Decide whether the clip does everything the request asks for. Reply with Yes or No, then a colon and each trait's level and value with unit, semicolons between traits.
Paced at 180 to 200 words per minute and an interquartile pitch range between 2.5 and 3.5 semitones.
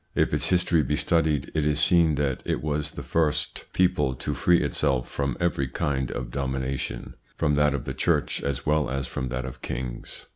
Yes: average, 195 wpm; average, 2.8 semitones